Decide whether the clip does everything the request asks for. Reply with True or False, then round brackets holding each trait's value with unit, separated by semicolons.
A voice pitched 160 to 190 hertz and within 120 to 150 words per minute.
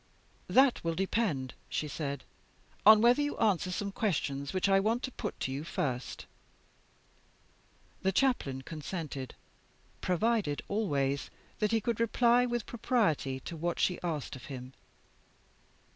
True (185 Hz; 135 wpm)